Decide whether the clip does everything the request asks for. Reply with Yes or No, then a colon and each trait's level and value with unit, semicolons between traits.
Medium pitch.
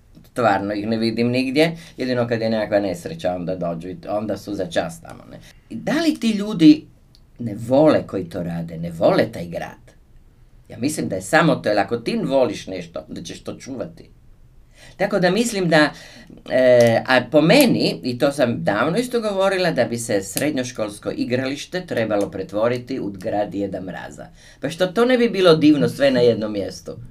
No: low, 125 Hz